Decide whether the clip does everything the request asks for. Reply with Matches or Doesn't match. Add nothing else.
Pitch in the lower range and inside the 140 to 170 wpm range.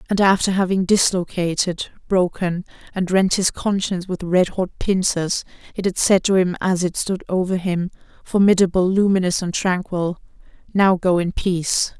Doesn't match